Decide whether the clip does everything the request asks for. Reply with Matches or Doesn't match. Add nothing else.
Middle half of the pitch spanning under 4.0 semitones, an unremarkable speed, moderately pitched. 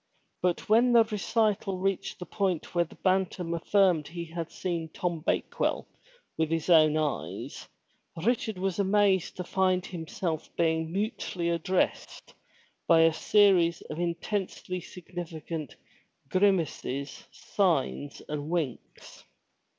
Doesn't match